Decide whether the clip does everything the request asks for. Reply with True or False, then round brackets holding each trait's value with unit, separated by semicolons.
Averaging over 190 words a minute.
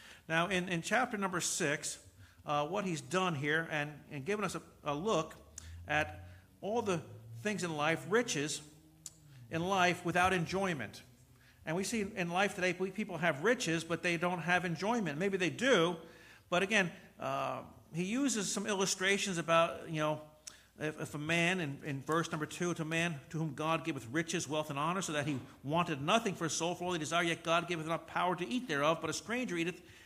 True (200 wpm)